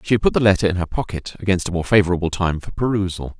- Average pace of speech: No, fast, 265 wpm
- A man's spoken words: Yes, male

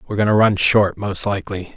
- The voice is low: Yes, low, 100 Hz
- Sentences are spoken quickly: Yes, fast, 275 wpm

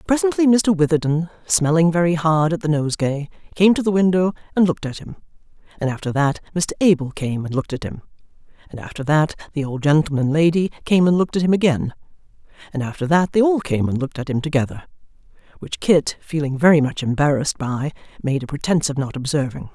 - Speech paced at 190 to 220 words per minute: Yes, average, 200 wpm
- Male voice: No, female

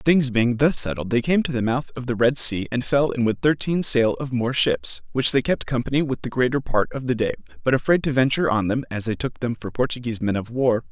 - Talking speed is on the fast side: Yes, fast, 265 wpm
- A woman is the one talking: No, male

